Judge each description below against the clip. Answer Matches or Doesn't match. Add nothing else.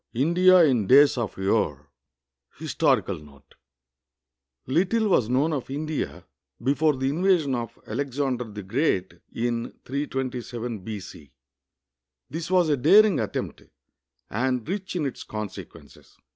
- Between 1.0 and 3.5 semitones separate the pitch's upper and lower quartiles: Doesn't match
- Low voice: Matches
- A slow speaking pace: Matches